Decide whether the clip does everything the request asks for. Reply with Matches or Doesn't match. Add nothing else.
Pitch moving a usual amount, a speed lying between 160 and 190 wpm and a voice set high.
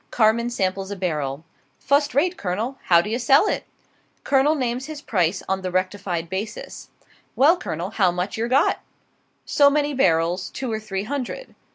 Doesn't match